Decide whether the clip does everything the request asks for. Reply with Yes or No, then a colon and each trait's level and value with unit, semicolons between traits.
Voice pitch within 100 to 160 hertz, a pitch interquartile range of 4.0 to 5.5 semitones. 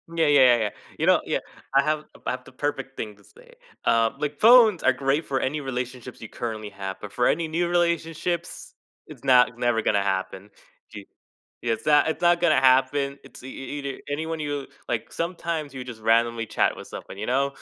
Yes: low, 135 Hz; average, 4.6 semitones